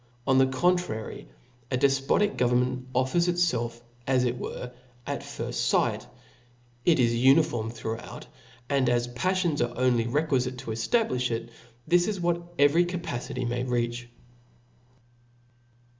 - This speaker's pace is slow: Yes, slow, 125 wpm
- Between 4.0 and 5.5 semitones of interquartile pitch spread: Yes, average, 4.8 semitones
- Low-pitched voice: Yes, low, 125 Hz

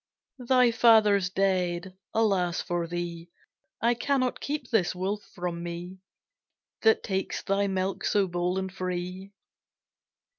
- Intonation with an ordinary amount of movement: Yes, average, 3.3 semitones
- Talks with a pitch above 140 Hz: Yes, high, 190 Hz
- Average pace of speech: No, slow, 120 wpm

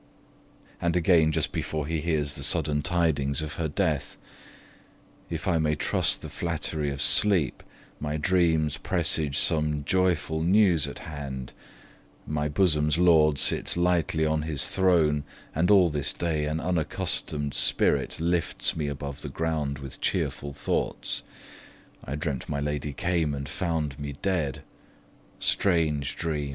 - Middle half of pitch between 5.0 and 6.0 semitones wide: No, narrow, 2.6 semitones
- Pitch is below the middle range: Yes, very low, 75 Hz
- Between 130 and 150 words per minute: Yes, average, 140 wpm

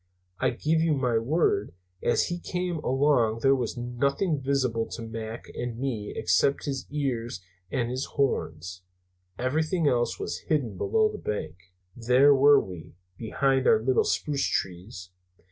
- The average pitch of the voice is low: Yes, low, 125 Hz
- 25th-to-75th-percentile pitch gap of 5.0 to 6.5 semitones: No, average, 3.9 semitones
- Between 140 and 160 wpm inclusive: Yes, average, 145 wpm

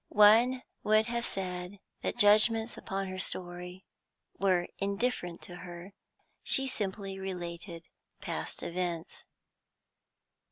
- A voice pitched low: No, high, 195 Hz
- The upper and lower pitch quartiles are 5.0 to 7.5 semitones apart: No, average, 3.3 semitones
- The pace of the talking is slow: Yes, slow, 105 wpm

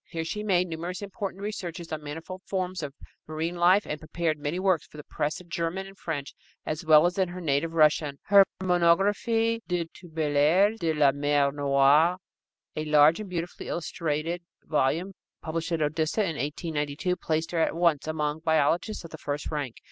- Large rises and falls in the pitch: No, average, 3.2 semitones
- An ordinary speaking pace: Yes, average, 180 wpm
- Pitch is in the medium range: Yes, medium, 165 Hz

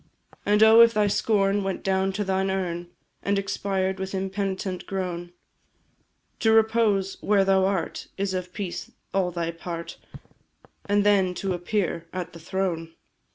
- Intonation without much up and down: Yes, narrow, 1.9 semitones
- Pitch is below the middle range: No, high, 190 Hz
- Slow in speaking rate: No, average, 150 wpm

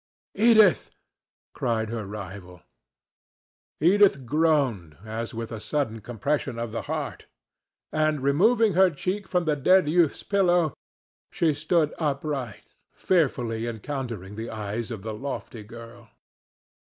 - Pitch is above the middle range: No, low, 130 Hz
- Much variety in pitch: Yes, wide, 6.3 semitones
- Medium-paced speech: No, slow, 120 wpm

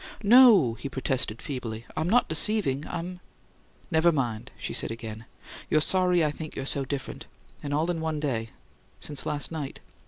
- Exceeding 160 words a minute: Yes, average, 180 wpm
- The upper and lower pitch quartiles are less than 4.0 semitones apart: No, average, 4.5 semitones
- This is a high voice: No, medium, 150 Hz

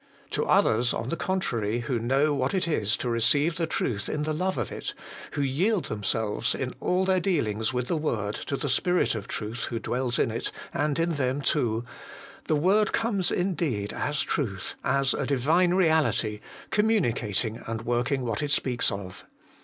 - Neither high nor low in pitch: No, low, 130 Hz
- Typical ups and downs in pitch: No, wide, 6.4 semitones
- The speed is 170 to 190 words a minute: Yes, average, 180 wpm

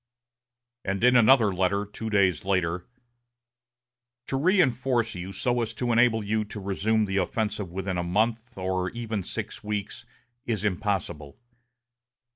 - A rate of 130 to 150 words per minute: Yes, slow, 135 wpm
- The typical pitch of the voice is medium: No, low, 105 Hz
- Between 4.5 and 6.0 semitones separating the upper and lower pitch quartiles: No, average, 3.4 semitones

